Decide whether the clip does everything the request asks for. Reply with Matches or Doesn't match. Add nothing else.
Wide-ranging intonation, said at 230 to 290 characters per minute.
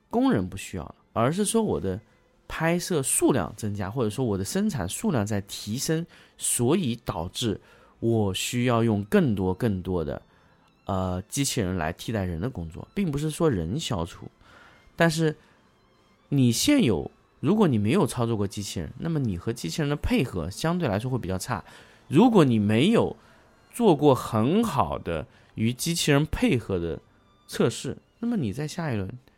Matches